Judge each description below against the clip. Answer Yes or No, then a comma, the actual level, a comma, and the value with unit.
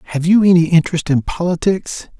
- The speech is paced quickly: No, average, 165 wpm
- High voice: No, medium, 170 Hz